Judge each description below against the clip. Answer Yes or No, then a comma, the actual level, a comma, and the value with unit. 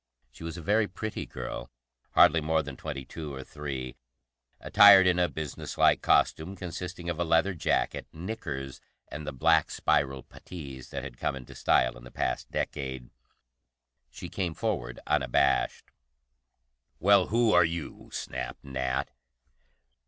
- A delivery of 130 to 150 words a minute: Yes, average, 145 wpm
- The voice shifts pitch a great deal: No, average, 4.9 semitones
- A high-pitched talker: No, very low, 80 Hz